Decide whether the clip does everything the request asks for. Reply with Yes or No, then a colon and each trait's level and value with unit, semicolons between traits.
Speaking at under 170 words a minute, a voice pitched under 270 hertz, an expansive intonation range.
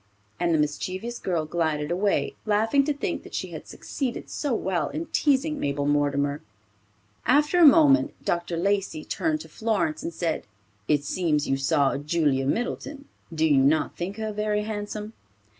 Yes: average, 160 wpm; medium, 185 Hz; wide, 7.9 semitones